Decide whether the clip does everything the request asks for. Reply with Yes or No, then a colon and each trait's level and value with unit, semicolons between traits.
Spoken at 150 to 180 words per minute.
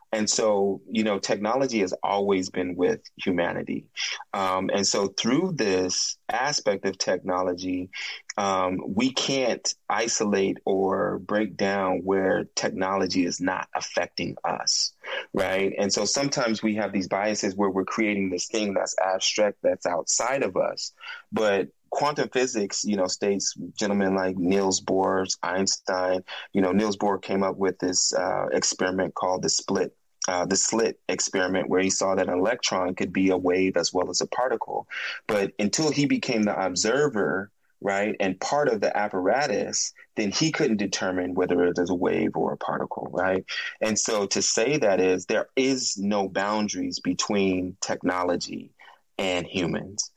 Yes: average, 160 wpm